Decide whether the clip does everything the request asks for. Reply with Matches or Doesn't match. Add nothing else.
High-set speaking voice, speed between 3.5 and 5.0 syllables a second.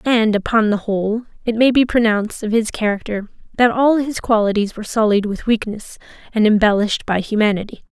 Doesn't match